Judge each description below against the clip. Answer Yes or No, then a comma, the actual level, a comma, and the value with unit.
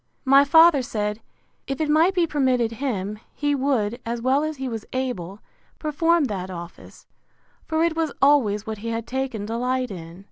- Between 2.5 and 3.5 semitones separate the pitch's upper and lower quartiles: No, wide, 5.4 semitones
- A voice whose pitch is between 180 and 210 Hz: No, very high, 255 Hz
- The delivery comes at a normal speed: Yes, average, 175 wpm